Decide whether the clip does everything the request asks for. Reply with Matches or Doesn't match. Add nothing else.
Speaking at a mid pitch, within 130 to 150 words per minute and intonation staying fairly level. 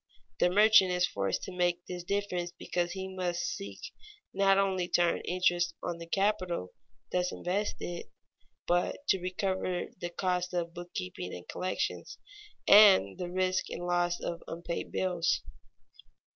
Matches